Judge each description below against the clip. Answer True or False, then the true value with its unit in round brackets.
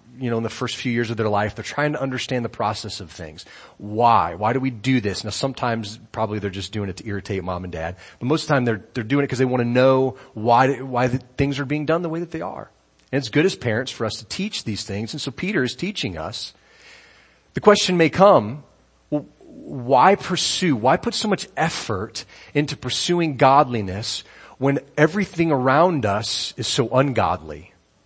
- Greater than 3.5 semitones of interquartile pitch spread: True (5.2 semitones)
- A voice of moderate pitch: False (125 Hz)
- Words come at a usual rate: False (215 wpm)